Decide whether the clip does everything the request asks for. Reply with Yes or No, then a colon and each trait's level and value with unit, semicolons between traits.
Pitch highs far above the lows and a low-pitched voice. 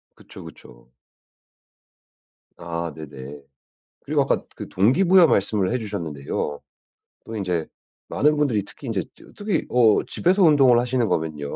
Yes: wide, 9.0 semitones; low, 105 Hz